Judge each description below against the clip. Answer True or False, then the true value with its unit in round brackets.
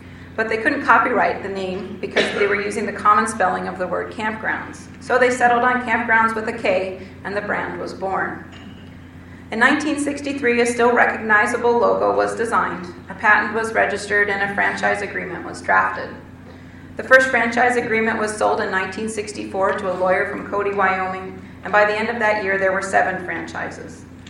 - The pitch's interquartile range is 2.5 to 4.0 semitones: True (3.5 semitones)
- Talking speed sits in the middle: True (180 wpm)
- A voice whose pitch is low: False (210 Hz)